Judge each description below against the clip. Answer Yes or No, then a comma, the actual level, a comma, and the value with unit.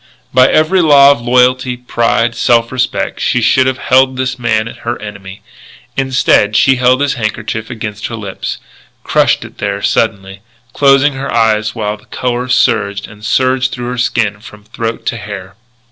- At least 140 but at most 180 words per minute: Yes, average, 165 wpm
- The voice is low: Yes, low, 120 Hz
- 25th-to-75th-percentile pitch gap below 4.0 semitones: Yes, average, 3.2 semitones